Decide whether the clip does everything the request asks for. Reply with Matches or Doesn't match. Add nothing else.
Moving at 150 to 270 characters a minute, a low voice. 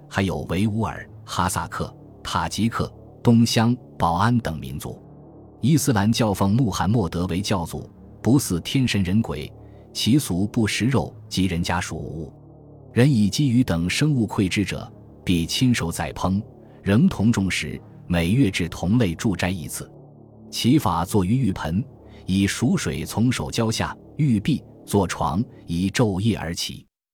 Matches